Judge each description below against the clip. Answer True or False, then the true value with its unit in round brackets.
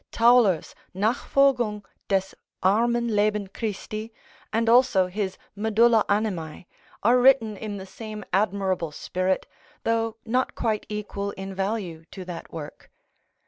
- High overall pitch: True (210 Hz)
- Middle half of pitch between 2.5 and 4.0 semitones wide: True (2.9 semitones)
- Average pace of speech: False (120 wpm)